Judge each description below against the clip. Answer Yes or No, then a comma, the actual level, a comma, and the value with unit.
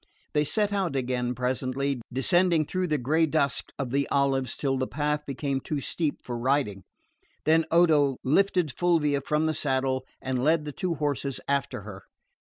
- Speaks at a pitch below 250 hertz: Yes, medium, 140 Hz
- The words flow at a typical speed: Yes, average, 170 wpm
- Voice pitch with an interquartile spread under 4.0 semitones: Yes, average, 3.2 semitones